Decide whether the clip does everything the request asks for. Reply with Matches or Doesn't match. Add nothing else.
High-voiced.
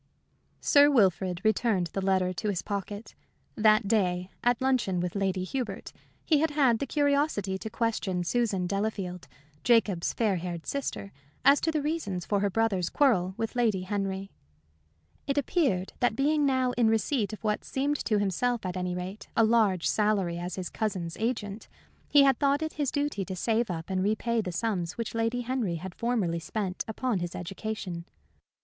Matches